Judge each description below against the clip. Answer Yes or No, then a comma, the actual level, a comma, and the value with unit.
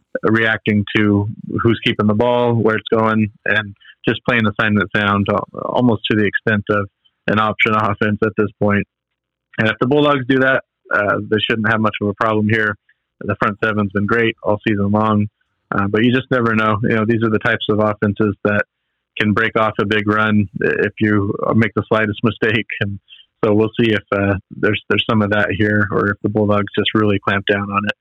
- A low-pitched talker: Yes, low, 110 Hz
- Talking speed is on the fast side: Yes, fast, 210 wpm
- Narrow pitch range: Yes, narrow, 1.4 semitones